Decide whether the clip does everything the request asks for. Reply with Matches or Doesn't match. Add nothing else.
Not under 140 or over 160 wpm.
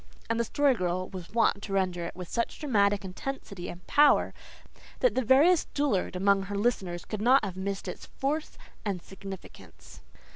Doesn't match